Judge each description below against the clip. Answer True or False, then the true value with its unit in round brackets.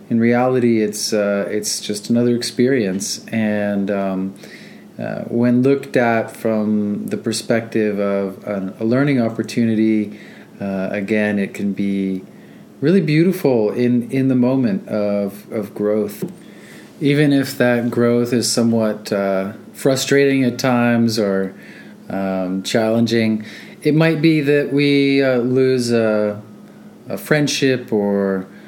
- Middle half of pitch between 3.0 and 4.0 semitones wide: True (3.7 semitones)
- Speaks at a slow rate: True (125 wpm)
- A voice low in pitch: True (115 Hz)